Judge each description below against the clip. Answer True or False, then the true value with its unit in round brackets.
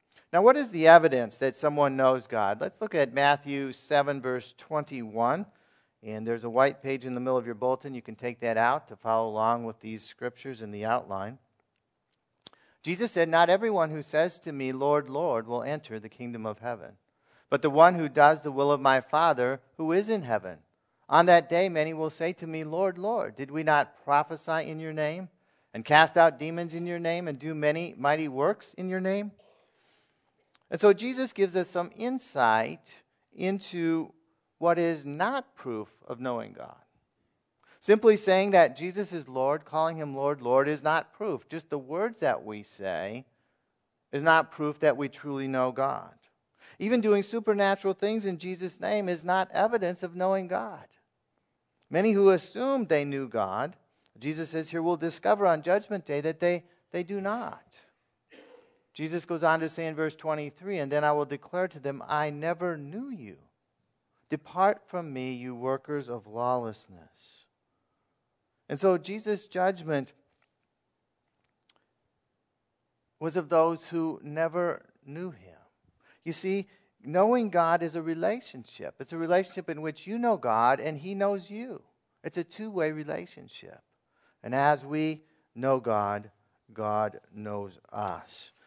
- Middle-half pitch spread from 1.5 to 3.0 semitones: False (5.3 semitones)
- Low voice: False (155 Hz)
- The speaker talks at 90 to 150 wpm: False (165 wpm)